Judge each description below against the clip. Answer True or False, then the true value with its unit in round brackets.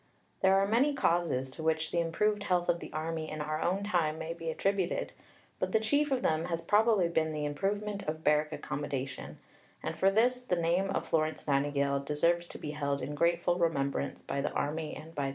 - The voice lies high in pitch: False (165 Hz)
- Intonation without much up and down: False (4.4 semitones)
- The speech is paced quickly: True (210 wpm)